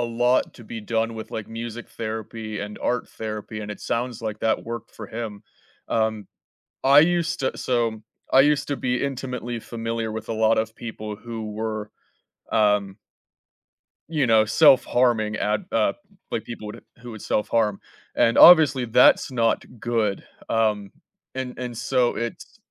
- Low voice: Yes, low, 115 Hz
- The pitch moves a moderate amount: No, narrow, 2.3 semitones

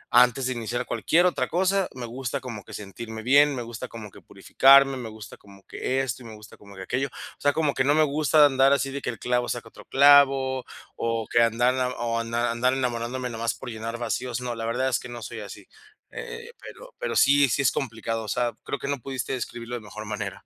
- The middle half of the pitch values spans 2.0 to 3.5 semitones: Yes, average, 2.9 semitones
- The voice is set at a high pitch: No, low, 125 Hz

